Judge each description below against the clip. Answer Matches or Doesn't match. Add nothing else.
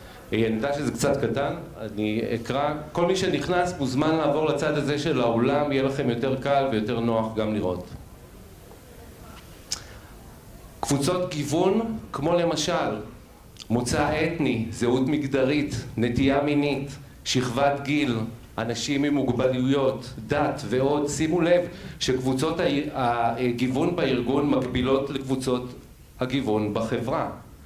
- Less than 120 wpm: Matches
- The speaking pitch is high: Doesn't match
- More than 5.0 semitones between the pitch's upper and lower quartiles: Doesn't match